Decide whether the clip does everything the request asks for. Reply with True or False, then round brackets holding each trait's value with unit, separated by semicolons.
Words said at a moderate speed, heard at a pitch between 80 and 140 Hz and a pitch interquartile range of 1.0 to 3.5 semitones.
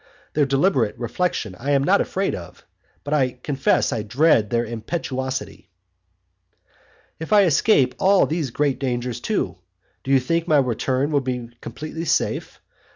False (150 wpm; 135 Hz; 4.1 semitones)